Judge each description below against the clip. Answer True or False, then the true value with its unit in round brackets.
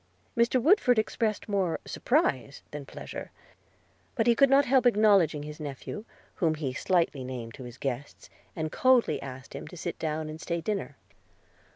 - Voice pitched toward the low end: False (165 Hz)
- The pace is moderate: True (165 wpm)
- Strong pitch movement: True (8.3 semitones)